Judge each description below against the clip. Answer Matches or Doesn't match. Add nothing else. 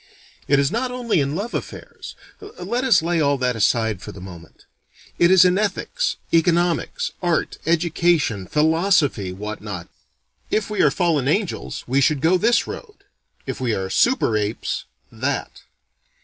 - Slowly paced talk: Doesn't match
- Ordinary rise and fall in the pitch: Doesn't match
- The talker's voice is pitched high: Doesn't match